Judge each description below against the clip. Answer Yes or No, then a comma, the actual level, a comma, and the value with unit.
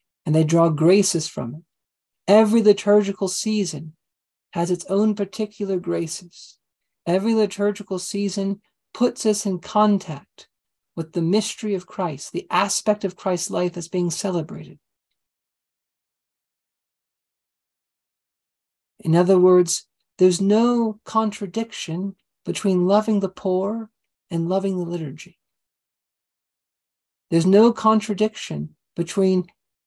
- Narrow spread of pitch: No, average, 3.5 semitones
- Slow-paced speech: Yes, slow, 105 wpm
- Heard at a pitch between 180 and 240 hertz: Yes, high, 190 Hz